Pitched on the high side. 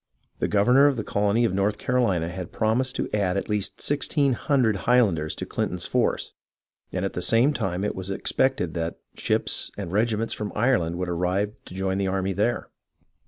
No: low, 100 Hz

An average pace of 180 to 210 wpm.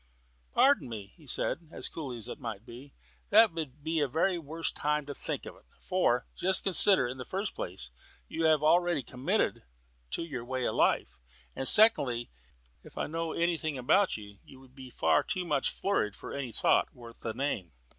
Yes: average, 195 wpm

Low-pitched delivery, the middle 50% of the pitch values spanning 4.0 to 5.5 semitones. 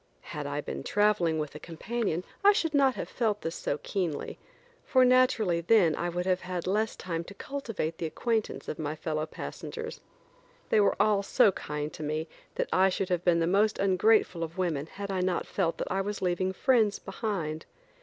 No: medium, 185 Hz; average, 4.4 semitones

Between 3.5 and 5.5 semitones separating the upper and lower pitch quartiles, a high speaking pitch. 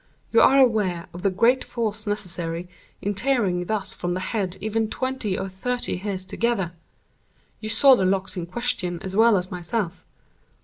Yes: average, 3.9 semitones; high, 200 Hz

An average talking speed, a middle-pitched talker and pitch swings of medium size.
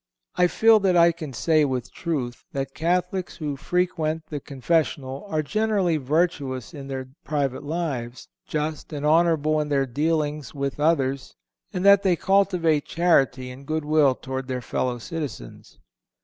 Yes: average, 150 wpm; medium, 150 Hz; average, 3.8 semitones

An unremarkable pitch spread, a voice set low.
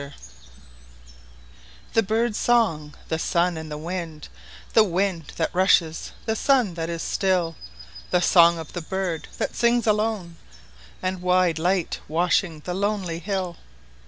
No: average, 4.2 semitones; medium, 170 Hz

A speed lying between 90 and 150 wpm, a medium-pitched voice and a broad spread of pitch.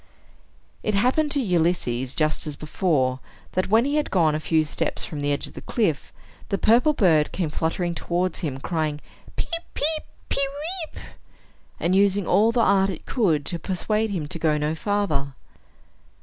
No: average, 175 wpm; medium, 180 Hz; wide, 5.9 semitones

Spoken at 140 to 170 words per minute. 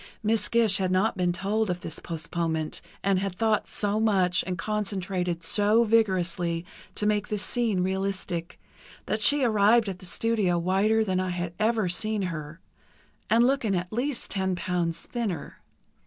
Yes: average, 160 wpm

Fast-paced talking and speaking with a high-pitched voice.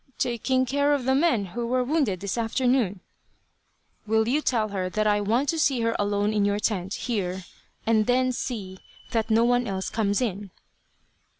No: average, 180 wpm; high, 225 Hz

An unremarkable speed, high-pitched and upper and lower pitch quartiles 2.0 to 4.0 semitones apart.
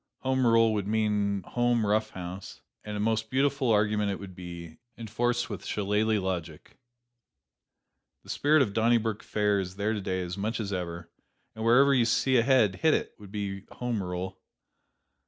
No: average, 170 wpm; low, 105 Hz; average, 3.1 semitones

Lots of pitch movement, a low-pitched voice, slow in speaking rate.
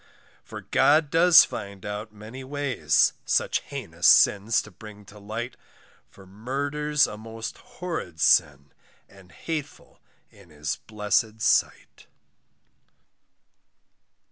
Yes: wide, 5.9 semitones; low, 110 Hz; slow, 110 wpm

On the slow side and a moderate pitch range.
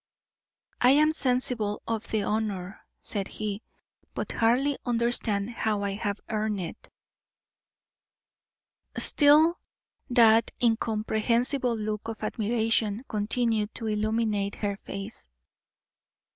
No: slow, 100 wpm; narrow, 2.2 semitones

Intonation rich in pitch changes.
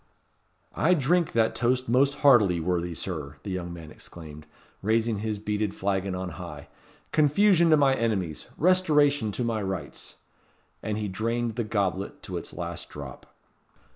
Yes: wide, 6.4 semitones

